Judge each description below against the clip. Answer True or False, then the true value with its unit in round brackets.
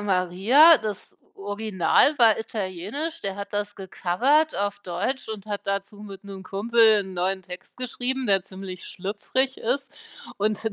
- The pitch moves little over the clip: False (3.6 semitones)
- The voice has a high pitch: True (205 Hz)